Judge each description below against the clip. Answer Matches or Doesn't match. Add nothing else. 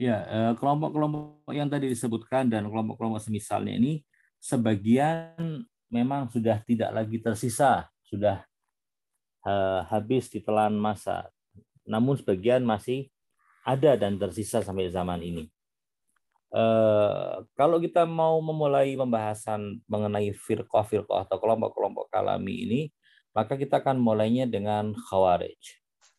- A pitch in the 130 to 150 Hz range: Doesn't match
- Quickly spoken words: Doesn't match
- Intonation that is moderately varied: Matches